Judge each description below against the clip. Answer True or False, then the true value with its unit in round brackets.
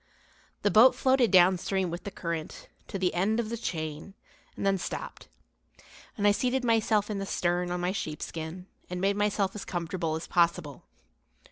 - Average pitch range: True (3.2 semitones)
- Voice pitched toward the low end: False (190 Hz)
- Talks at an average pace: True (170 wpm)